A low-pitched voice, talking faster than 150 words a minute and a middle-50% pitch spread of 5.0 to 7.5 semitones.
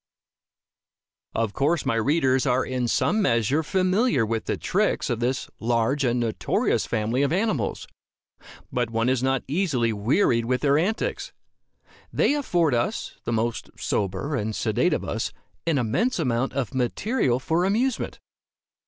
No: low, 130 Hz; average, 145 wpm; wide, 5.6 semitones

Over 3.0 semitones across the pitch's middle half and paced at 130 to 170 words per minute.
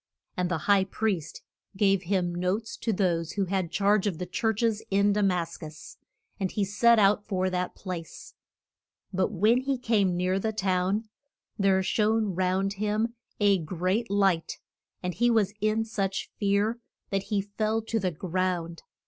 No: average, 2.7 semitones; average, 165 wpm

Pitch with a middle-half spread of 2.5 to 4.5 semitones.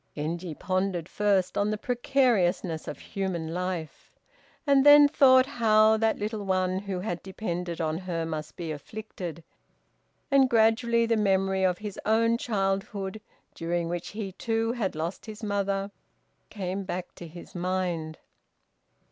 Yes: average, 4.0 semitones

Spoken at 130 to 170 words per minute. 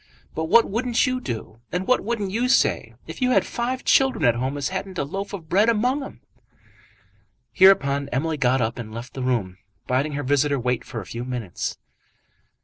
No: average, 195 wpm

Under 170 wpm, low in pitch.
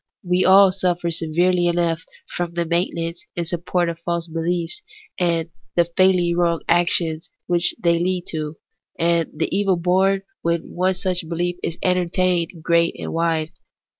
No: average, 155 wpm; medium, 170 Hz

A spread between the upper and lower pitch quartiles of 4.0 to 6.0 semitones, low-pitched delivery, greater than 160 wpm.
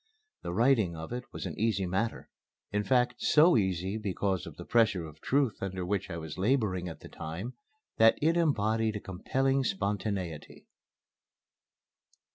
No: average, 4.7 semitones; low, 105 Hz; average, 155 wpm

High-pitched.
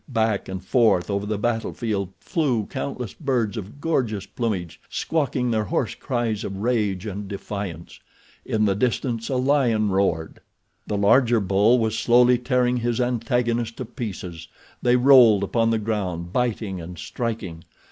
No: low, 110 Hz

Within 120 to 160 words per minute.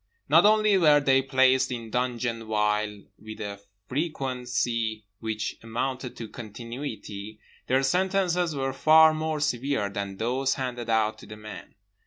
Yes: average, 140 wpm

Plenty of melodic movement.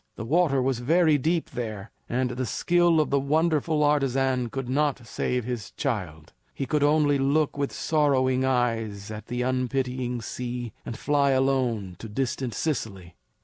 No: average, 3.3 semitones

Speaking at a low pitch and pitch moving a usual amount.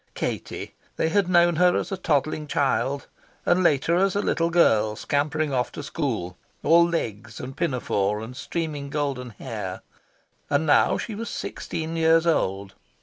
No: medium, 150 Hz; average, 4.9 semitones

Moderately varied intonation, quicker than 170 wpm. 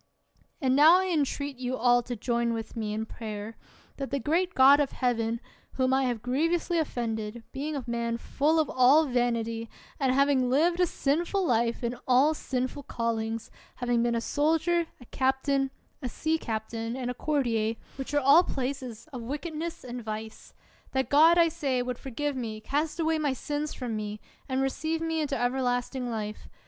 Yes: average, 3.9 semitones; average, 180 wpm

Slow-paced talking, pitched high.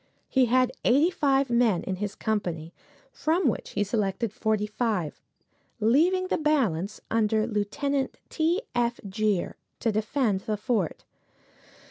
Yes: slow, 130 wpm; high, 220 Hz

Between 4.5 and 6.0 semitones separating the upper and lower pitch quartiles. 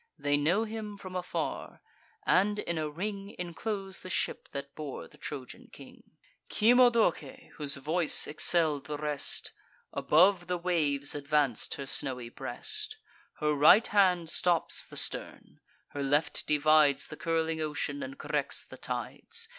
Yes: wide, 5.4 semitones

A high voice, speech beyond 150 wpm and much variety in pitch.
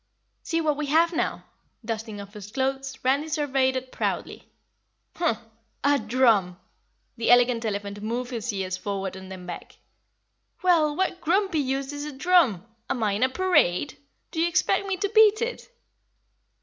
Yes: very high, 260 Hz; average, 160 wpm; wide, 6.9 semitones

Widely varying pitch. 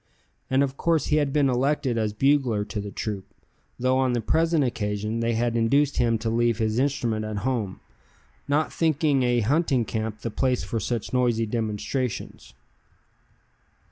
No: average, 3.7 semitones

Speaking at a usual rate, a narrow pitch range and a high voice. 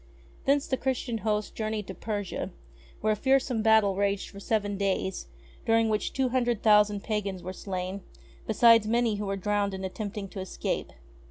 Yes: average, 170 wpm; narrow, 2.3 semitones; high, 210 Hz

